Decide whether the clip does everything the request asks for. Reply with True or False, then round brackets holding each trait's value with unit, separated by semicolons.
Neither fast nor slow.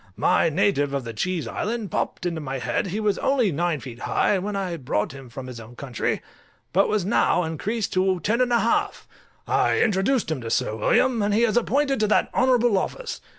False (215 wpm)